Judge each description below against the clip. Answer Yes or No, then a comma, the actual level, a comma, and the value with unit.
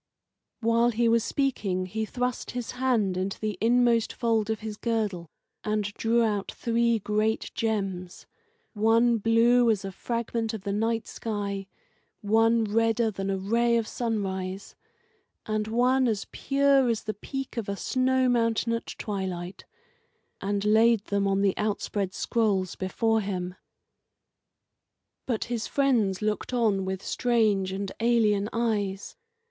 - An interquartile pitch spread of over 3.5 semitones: No, average, 2.7 semitones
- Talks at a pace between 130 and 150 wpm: Yes, average, 140 wpm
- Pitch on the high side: Yes, high, 220 Hz